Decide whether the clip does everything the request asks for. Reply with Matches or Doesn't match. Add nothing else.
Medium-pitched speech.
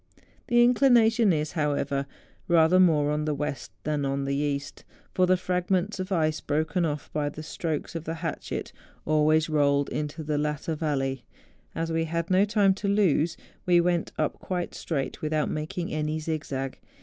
Matches